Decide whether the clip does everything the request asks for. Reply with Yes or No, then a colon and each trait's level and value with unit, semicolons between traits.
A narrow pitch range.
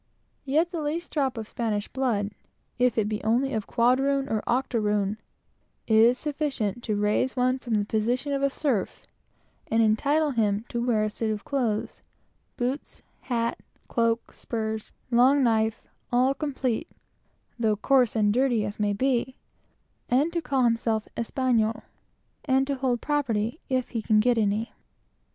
No: average, 3.6 semitones